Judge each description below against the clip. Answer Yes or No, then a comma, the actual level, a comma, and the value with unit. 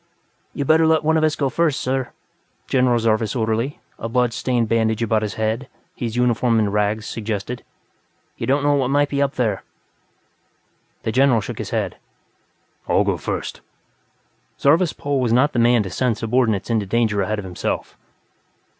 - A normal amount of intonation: Yes, average, 3.7 semitones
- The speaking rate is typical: Yes, average, 170 wpm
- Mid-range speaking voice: No, low, 120 Hz